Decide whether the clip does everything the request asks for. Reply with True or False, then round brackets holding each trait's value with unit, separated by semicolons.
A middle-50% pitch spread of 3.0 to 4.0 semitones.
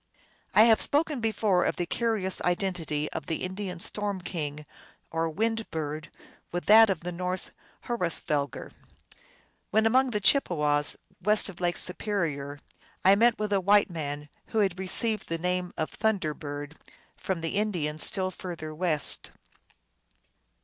False (4.9 semitones)